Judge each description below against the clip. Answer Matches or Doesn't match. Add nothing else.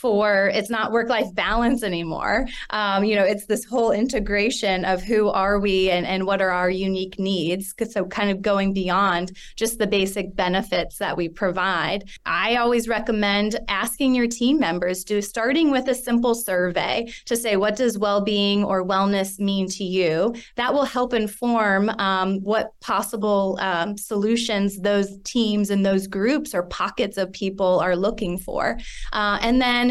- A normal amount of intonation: Matches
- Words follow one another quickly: Doesn't match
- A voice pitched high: Matches